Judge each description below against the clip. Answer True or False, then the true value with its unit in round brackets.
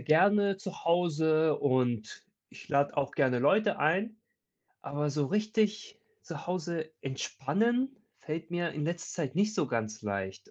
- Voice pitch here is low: False (160 Hz)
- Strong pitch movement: True (6.2 semitones)